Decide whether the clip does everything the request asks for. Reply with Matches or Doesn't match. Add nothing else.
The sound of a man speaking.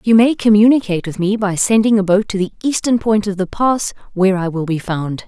Doesn't match